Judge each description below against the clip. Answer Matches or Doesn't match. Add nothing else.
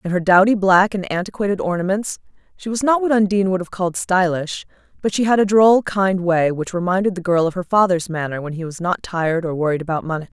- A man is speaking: Doesn't match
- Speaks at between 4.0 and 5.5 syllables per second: Doesn't match